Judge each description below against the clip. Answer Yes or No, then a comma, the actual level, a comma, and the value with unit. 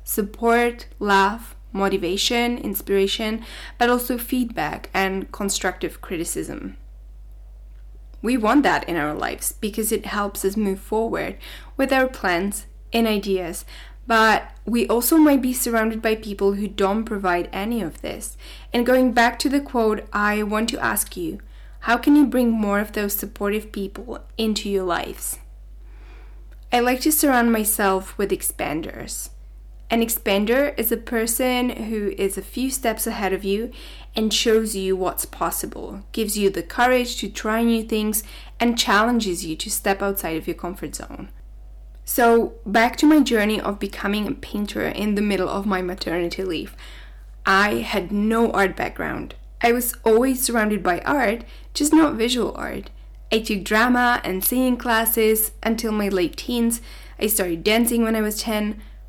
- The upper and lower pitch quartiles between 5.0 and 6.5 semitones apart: No, average, 3.3 semitones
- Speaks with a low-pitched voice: No, high, 215 Hz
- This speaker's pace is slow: No, average, 155 wpm